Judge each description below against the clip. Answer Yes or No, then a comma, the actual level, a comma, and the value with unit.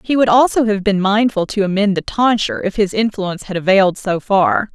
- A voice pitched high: Yes, high, 200 Hz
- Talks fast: Yes, fast, 215 wpm